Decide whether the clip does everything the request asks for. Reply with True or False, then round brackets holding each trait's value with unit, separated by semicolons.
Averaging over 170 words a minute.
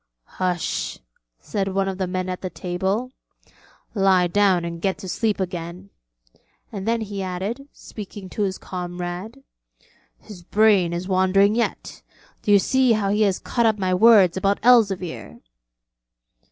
False (150 wpm)